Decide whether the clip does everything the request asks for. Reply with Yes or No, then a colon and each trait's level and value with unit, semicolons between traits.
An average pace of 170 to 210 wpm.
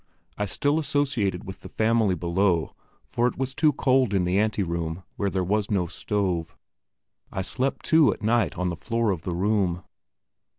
Yes: average, 180 wpm